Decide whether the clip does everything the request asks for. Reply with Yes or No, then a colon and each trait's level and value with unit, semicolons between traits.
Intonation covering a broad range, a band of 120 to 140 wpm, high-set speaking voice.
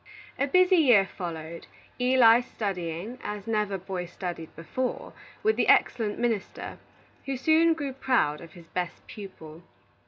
Yes: wide, 6.7 semitones; slow, 135 wpm; high, 210 Hz